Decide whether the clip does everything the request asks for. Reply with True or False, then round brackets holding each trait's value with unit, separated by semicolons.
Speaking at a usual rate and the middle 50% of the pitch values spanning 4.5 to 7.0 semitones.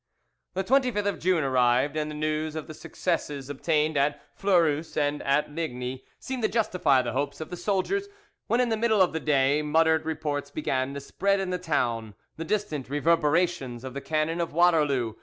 False (190 wpm; 4.0 semitones)